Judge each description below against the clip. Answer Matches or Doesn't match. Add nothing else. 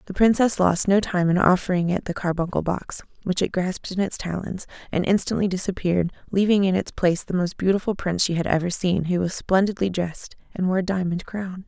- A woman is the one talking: Matches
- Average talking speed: Doesn't match